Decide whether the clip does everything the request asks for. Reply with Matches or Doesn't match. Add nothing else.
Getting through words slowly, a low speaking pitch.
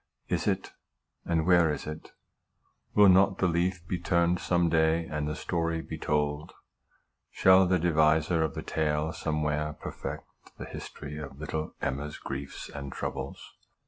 Doesn't match